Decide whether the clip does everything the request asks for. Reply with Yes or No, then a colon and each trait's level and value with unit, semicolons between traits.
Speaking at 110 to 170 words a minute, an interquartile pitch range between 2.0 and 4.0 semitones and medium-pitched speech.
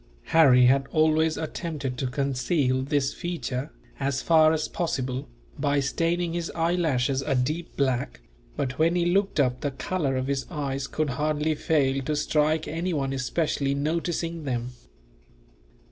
Yes: average, 145 wpm; average, 3.4 semitones; medium, 145 Hz